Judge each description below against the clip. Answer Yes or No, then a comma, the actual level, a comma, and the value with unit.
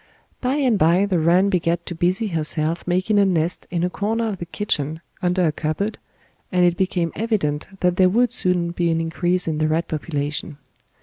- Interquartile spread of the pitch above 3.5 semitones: No, average, 3.0 semitones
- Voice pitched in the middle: Yes, medium, 175 Hz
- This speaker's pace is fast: No, average, 195 wpm